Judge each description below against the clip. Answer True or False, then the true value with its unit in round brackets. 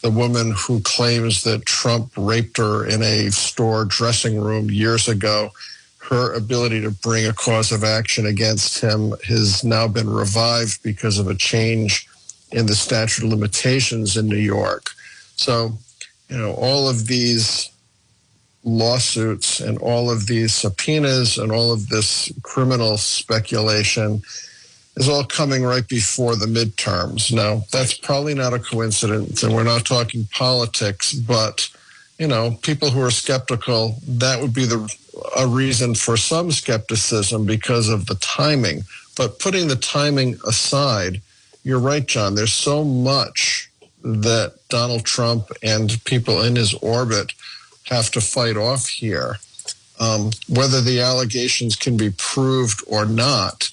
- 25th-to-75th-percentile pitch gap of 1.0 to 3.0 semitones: True (2.5 semitones)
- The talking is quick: False (145 wpm)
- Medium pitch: False (115 Hz)